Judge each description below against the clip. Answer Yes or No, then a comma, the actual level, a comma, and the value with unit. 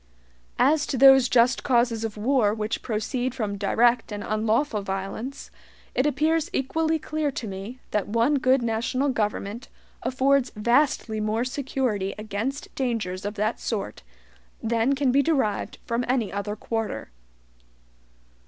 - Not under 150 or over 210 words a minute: No, slow, 135 wpm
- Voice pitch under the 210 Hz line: No, high, 235 Hz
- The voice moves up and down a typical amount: Yes, average, 3.9 semitones